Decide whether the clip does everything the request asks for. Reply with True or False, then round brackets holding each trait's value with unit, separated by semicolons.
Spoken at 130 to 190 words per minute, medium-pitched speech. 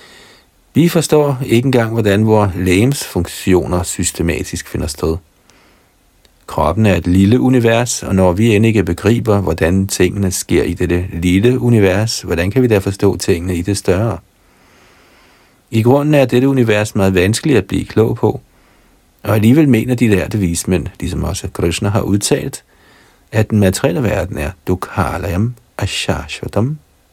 False (150 wpm; 100 Hz)